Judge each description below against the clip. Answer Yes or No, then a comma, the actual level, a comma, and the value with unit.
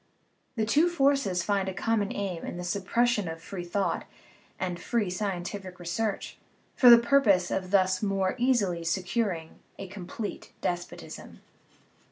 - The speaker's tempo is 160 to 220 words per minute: No, average, 140 wpm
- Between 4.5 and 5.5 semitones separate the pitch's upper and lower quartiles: No, average, 3.9 semitones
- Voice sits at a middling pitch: No, high, 195 Hz